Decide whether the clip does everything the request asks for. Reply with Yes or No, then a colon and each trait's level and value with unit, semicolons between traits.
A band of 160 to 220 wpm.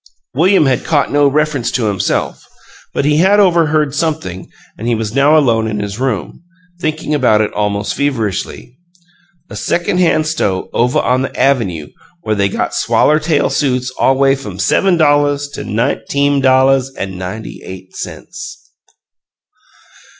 No: average, 150 wpm